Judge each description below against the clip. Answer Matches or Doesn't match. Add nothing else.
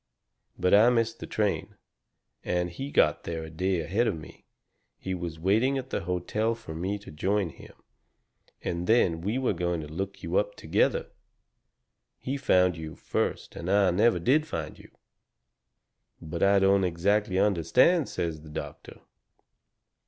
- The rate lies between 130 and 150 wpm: Doesn't match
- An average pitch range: Matches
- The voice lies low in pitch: Matches